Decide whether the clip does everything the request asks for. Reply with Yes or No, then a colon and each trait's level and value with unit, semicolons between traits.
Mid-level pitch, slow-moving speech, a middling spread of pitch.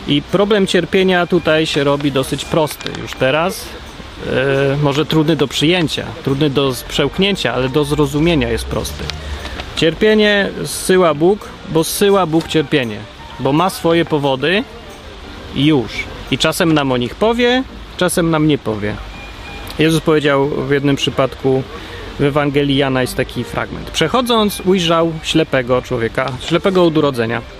No: medium, 145 Hz; average, 140 wpm; average, 4.6 semitones